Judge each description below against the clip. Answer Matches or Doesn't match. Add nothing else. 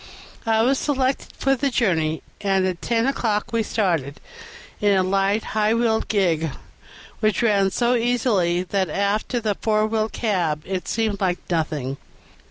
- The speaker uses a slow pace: Doesn't match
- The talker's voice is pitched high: Matches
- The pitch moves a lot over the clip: Doesn't match